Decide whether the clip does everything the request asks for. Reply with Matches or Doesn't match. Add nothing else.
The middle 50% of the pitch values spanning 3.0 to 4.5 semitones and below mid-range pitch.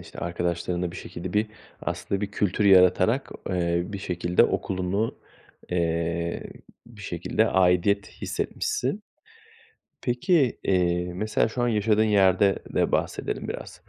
Matches